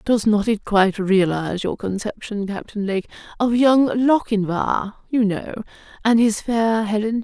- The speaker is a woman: Yes, female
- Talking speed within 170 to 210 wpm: No, average, 150 wpm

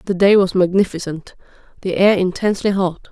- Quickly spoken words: No, average, 155 wpm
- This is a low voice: No, medium, 185 Hz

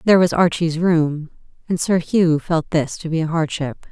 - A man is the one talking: No, female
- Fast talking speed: Yes, fast, 215 wpm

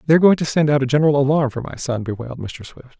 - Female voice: No, male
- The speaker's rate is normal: No, fast, 300 wpm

